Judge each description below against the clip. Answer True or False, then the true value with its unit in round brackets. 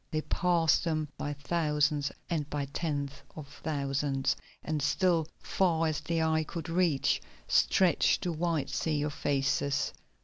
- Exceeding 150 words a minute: False (140 wpm)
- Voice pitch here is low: False (155 Hz)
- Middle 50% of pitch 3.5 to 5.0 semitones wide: False (2.4 semitones)